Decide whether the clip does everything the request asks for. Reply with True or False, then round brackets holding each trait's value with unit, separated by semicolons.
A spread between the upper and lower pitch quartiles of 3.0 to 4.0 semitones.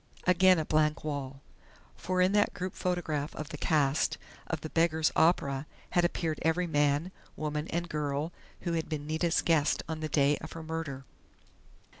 False (2.5 semitones)